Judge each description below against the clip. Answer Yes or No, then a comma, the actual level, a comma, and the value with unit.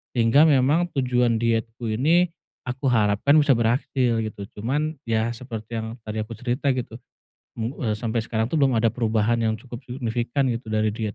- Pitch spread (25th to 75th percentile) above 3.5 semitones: No, average, 2.8 semitones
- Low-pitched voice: Yes, low, 120 Hz